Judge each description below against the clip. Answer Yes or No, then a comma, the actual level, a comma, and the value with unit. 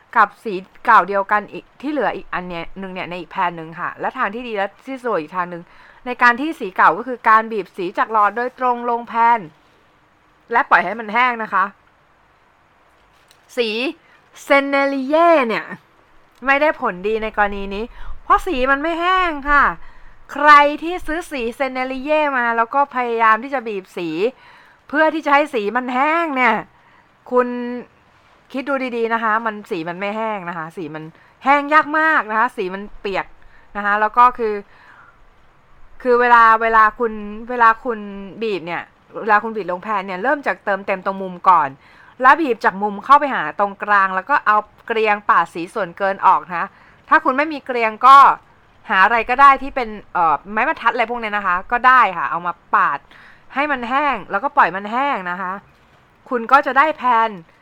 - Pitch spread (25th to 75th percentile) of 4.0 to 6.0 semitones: Yes, average, 5.1 semitones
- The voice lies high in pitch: Yes, high, 235 Hz